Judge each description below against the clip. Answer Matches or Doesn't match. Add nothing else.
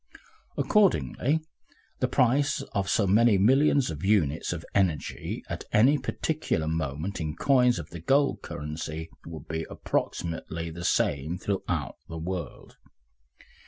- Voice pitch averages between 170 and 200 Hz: Doesn't match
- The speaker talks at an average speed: Doesn't match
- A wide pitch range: Matches